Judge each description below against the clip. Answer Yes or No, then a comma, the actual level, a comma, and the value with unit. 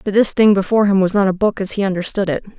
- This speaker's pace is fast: Yes, fast, 300 wpm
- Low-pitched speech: No, high, 195 Hz